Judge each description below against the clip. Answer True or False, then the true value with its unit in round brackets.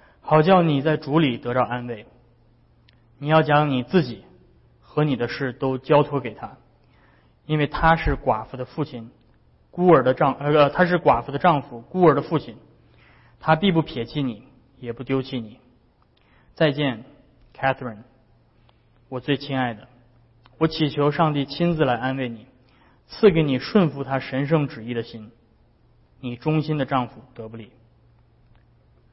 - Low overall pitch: True (130 Hz)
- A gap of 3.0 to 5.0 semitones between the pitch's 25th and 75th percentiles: True (3.9 semitones)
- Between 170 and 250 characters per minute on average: True (230 characters per minute)